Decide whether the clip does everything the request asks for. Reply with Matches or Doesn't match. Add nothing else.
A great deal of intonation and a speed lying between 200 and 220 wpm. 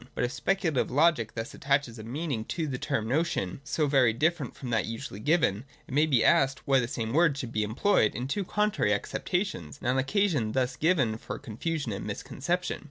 Matches